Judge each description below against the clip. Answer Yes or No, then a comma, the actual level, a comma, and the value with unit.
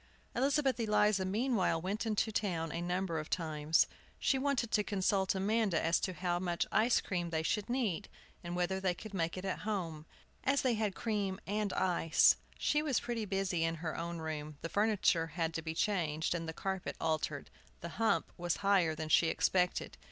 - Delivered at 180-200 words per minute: Yes, average, 190 wpm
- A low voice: No, medium, 185 Hz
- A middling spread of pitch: Yes, average, 4.3 semitones